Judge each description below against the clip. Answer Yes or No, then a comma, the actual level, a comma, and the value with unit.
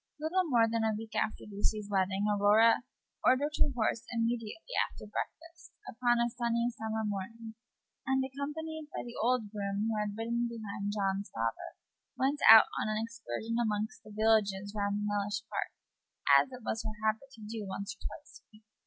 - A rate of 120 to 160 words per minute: No, average, 175 wpm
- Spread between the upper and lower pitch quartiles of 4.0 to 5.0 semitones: No, narrow, 2.5 semitones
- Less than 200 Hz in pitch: No, high, 220 Hz